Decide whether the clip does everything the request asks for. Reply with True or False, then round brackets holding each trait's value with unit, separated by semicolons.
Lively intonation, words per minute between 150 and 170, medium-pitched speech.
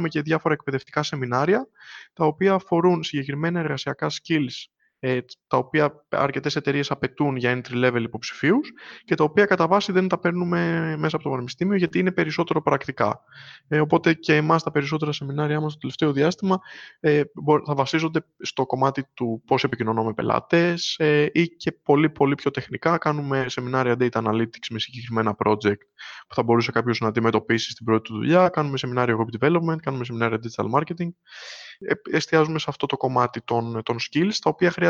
False (4.8 semitones; 165 wpm; 145 Hz)